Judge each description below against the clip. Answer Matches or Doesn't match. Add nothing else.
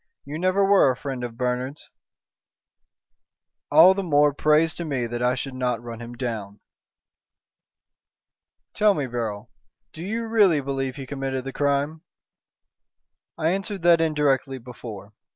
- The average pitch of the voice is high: Doesn't match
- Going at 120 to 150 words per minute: Matches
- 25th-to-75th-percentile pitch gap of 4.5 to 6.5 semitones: Matches